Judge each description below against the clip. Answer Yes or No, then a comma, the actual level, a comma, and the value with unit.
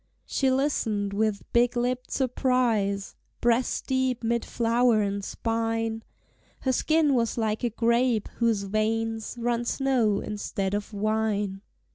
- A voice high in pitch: Yes, high, 230 Hz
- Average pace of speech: No, slow, 125 wpm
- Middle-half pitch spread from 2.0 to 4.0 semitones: Yes, narrow, 2.6 semitones